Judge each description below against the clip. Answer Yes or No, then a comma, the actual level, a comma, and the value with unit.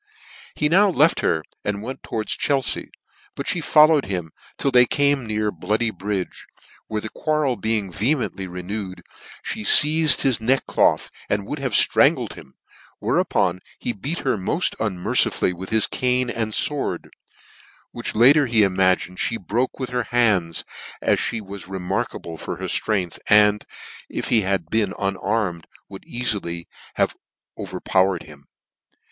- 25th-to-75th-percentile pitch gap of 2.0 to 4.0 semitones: No, average, 5.1 semitones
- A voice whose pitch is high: No, low, 110 Hz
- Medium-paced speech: Yes, average, 150 wpm